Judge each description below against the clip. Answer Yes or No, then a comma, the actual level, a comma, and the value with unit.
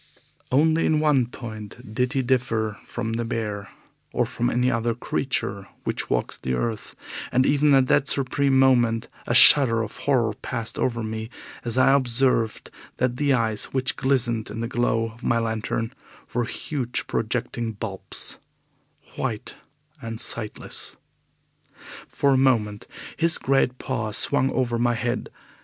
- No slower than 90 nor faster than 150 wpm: Yes, average, 145 wpm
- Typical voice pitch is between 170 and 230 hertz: No, low, 120 Hz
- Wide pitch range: No, average, 2.7 semitones